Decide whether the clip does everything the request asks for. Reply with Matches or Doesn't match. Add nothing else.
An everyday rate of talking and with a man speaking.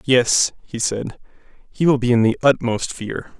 Matches